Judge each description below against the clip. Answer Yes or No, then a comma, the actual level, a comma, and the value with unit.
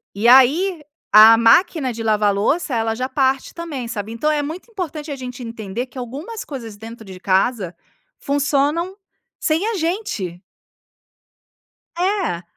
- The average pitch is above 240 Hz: Yes, very high, 260 Hz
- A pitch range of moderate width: No, wide, 6.1 semitones